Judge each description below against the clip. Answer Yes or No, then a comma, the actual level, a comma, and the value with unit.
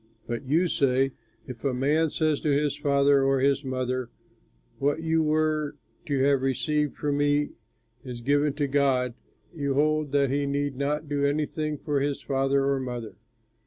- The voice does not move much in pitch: Yes, narrow, 1.7 semitones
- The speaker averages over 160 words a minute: Yes, average, 170 wpm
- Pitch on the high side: No, medium, 140 Hz